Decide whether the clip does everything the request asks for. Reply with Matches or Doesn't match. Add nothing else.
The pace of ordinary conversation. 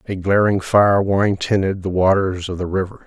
Matches